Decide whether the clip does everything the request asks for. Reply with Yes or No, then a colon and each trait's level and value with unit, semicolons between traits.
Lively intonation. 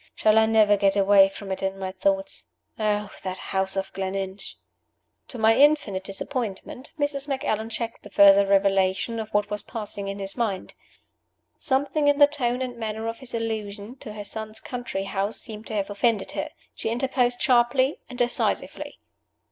No: average, 3.7 semitones